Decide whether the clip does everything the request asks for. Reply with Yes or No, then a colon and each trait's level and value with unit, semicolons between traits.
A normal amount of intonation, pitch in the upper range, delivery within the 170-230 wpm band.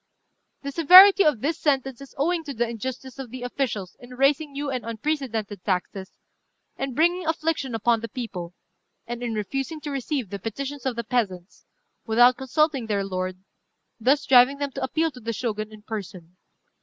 Yes: average, 4.3 semitones; very high, 250 Hz; average, 175 wpm